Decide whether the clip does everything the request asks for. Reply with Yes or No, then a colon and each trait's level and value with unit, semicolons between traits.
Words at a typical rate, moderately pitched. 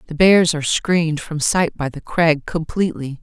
Yes: average, 185 wpm; medium, 160 Hz